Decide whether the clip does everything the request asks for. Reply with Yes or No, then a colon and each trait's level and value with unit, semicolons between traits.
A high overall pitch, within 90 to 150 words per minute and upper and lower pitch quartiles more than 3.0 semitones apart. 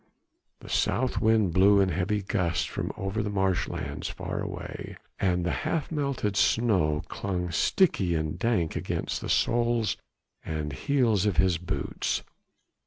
No: very low, 95 Hz; average, 140 wpm; average, 4.1 semitones